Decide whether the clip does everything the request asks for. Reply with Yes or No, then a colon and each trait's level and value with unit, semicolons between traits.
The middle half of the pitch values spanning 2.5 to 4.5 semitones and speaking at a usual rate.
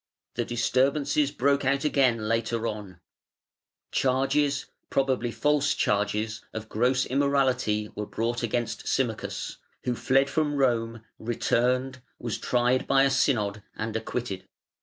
No: average, 3.3 semitones; slow, 120 wpm